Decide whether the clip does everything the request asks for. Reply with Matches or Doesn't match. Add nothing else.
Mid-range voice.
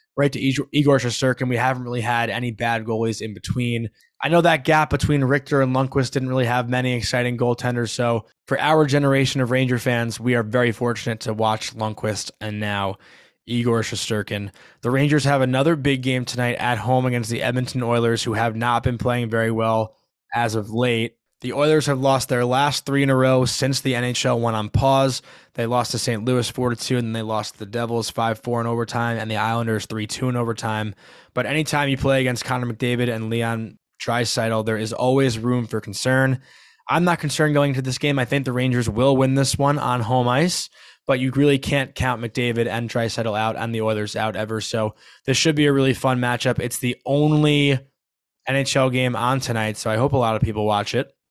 Doesn't match